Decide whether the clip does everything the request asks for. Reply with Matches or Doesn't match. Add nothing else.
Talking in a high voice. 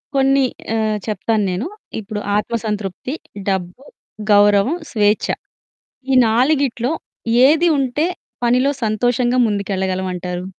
Matches